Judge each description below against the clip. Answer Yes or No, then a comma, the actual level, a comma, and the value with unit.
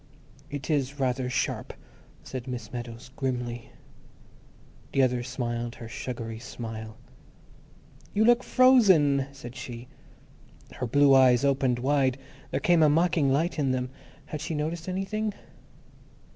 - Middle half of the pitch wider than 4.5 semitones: No, average, 3.9 semitones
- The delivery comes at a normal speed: No, slow, 130 wpm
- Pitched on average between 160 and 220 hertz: No, low, 135 Hz